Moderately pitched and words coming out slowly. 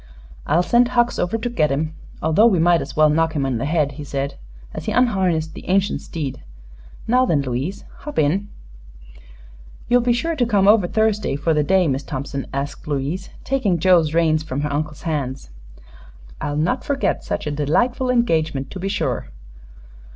No: medium, 165 Hz; average, 180 wpm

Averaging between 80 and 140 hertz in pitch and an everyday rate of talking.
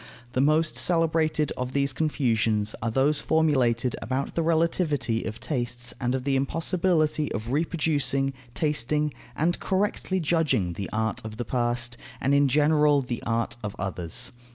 Yes: low, 135 Hz; average, 150 wpm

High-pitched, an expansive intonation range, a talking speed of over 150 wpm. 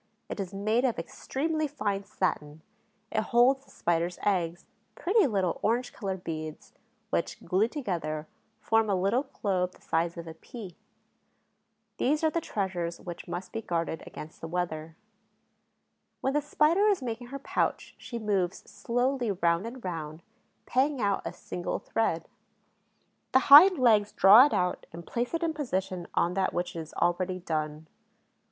Yes: high, 195 Hz; wide, 6.6 semitones; average, 160 wpm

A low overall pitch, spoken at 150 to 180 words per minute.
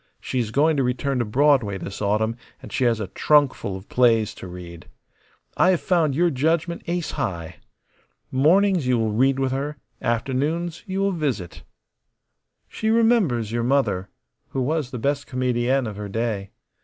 Yes: low, 130 Hz; average, 170 wpm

